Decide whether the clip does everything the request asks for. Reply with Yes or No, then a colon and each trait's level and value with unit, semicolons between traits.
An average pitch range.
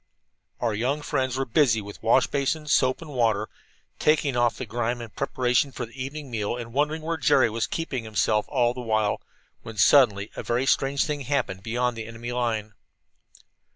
Yes: average, 3.5 semitones